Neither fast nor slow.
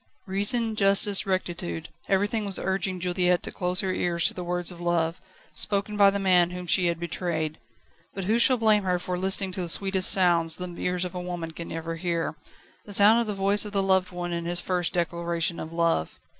No: fast, 210 wpm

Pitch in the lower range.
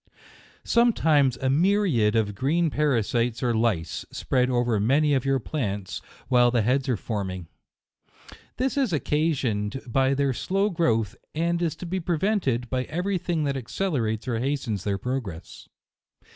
Yes: low, 130 Hz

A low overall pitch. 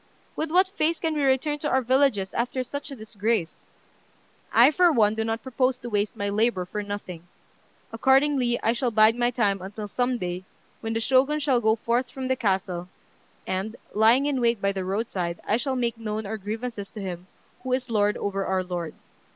No: high, 225 Hz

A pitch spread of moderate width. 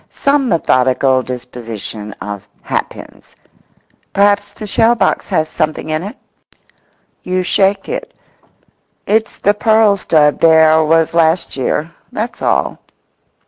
No: wide, 5.7 semitones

